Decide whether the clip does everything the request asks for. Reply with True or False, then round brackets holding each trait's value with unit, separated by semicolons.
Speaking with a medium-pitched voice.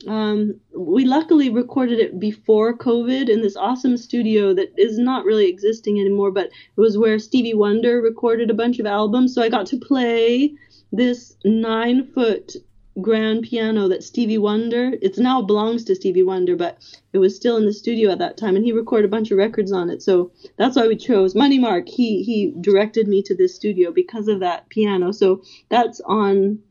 False (225 Hz)